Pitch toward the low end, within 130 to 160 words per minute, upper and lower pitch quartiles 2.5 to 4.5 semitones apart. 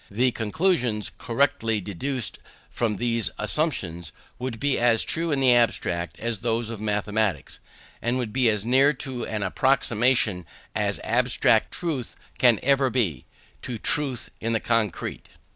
Yes: low, 115 Hz; average, 140 wpm; average, 3.5 semitones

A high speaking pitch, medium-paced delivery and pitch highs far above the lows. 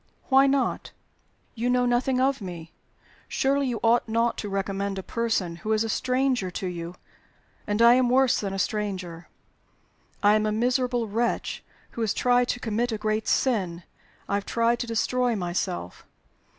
No: high, 225 Hz; average, 170 wpm; average, 3.9 semitones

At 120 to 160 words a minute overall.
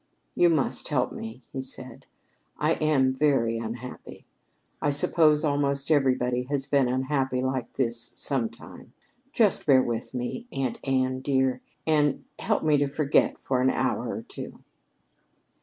Yes: average, 140 wpm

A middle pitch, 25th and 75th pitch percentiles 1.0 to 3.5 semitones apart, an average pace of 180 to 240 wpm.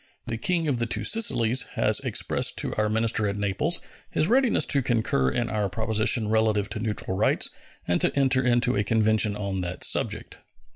No: low, 110 Hz; average, 3.2 semitones; average, 185 wpm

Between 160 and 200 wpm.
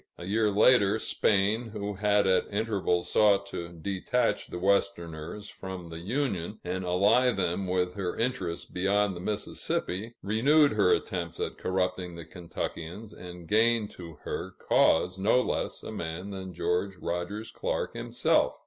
No: average, 150 wpm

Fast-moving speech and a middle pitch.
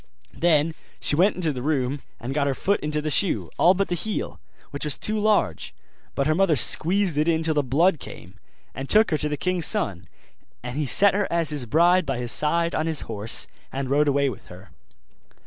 Yes: fast, 215 wpm; medium, 150 Hz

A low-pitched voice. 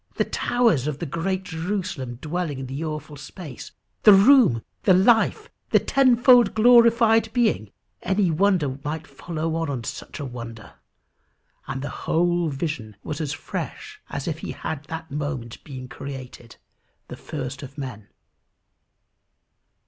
No: medium, 160 Hz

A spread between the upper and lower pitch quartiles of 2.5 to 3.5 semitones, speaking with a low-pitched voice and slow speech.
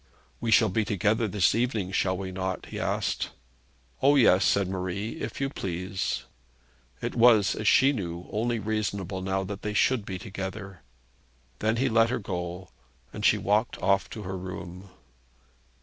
No: average, 3.0 semitones; low, 100 Hz; average, 165 wpm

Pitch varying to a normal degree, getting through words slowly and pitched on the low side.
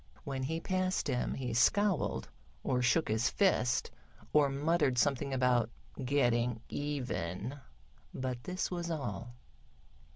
Yes: average, 4.4 semitones; slow, 120 wpm; low, 130 Hz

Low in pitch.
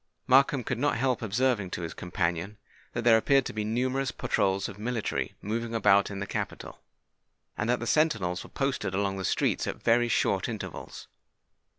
Yes: low, 115 Hz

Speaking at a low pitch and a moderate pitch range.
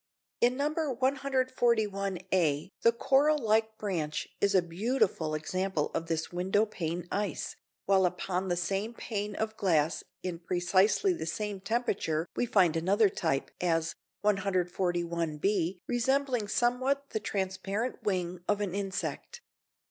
No: high, 195 Hz; average, 4.3 semitones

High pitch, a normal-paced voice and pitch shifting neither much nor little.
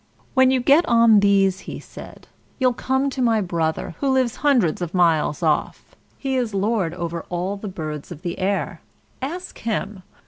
No: high, 200 Hz; average, 180 wpm; wide, 6.6 semitones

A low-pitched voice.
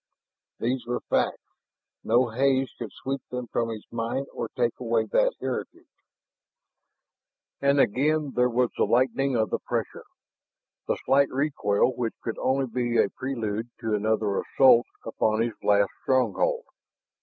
Yes: low, 125 Hz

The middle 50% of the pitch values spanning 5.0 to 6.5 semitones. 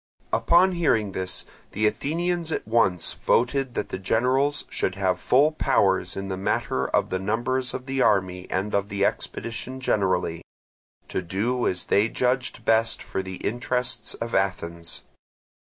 Yes: average, 5.3 semitones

